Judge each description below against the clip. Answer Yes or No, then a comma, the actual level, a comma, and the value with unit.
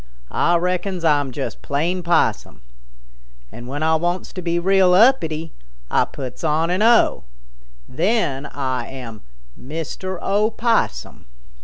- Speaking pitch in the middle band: Yes, medium, 170 Hz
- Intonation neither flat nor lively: Yes, average, 4.6 semitones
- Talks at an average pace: No, slow, 120 wpm